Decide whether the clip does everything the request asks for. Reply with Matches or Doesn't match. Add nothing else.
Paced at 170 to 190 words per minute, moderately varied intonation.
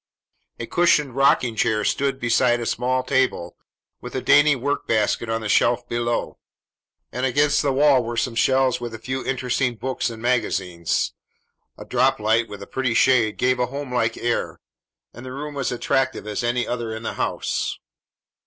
Doesn't match